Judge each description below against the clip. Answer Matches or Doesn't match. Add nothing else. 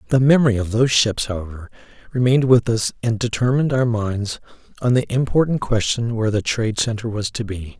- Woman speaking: Doesn't match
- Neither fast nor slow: Matches